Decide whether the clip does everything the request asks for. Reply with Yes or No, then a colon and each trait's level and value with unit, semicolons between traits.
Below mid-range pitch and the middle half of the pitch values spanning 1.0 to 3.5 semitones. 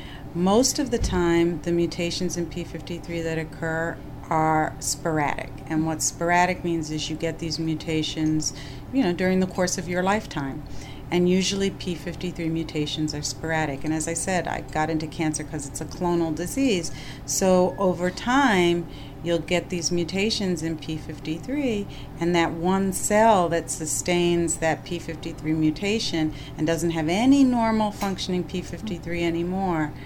No: medium, 165 Hz; narrow, 2.5 semitones